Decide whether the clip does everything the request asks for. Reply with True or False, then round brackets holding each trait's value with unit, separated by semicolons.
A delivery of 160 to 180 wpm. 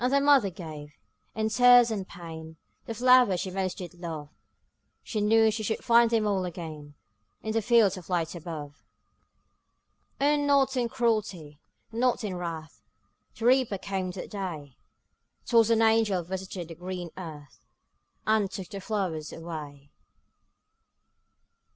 False (145 wpm)